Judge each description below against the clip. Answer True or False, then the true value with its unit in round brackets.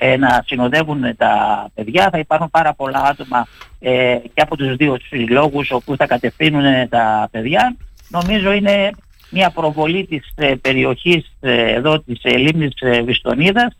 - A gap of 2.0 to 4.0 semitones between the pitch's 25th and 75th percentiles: False (4.4 semitones)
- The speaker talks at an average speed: True (150 wpm)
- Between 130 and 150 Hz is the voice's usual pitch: True (140 Hz)